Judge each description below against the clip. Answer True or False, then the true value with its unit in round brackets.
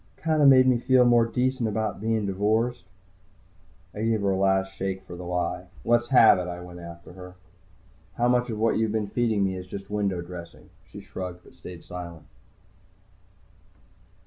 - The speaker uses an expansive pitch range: False (4.4 semitones)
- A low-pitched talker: True (100 Hz)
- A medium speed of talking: True (180 wpm)